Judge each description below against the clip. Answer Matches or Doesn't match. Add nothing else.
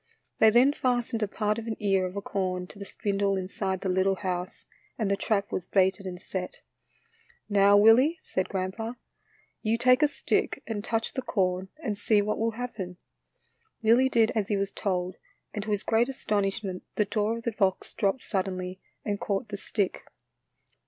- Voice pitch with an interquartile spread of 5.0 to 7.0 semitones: Doesn't match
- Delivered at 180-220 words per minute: Matches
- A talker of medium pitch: Doesn't match